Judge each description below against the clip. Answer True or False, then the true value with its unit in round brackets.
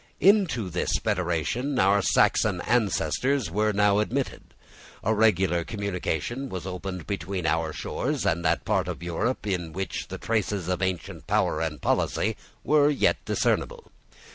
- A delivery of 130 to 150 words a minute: True (140 wpm)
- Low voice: True (100 Hz)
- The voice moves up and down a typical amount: True (4.8 semitones)